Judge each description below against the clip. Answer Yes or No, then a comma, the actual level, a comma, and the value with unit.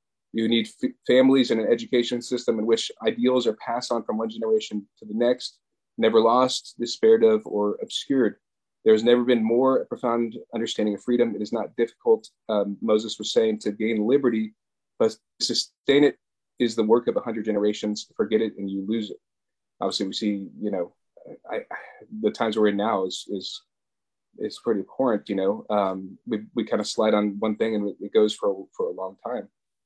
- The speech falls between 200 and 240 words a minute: Yes, fast, 205 wpm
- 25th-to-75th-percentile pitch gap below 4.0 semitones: Yes, average, 2.7 semitones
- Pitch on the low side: Yes, low, 115 Hz